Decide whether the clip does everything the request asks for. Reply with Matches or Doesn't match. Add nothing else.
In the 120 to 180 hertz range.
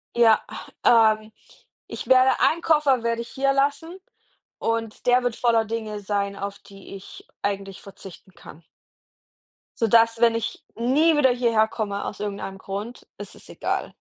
Doesn't match